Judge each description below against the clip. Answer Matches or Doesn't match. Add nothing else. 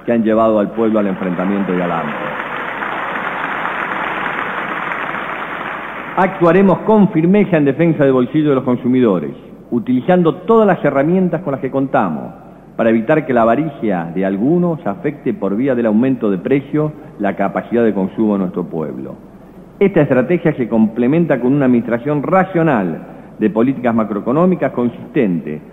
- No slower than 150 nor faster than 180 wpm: Doesn't match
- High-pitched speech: Doesn't match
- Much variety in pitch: Matches